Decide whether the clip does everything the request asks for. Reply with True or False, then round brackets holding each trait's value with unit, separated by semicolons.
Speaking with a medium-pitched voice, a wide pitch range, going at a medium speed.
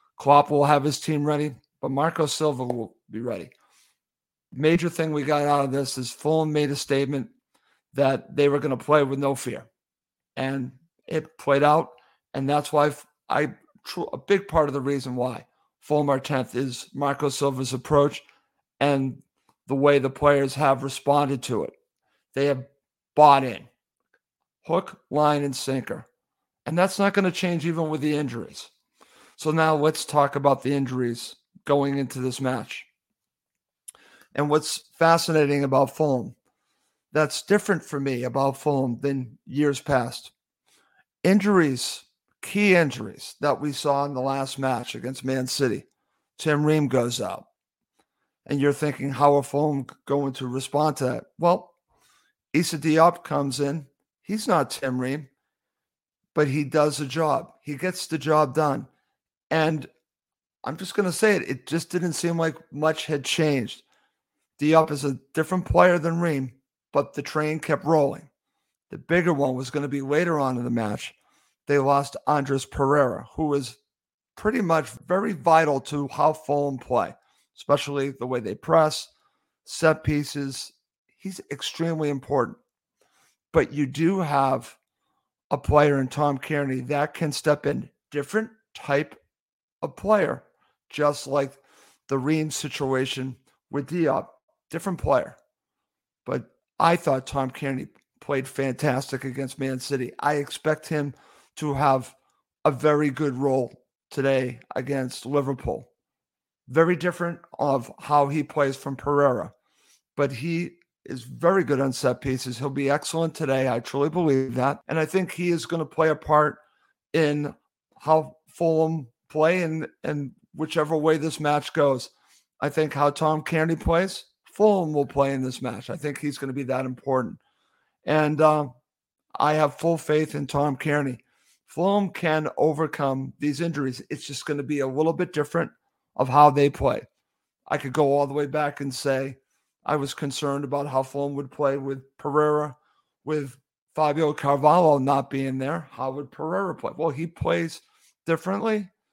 False (145 Hz; 2.5 semitones; 155 wpm)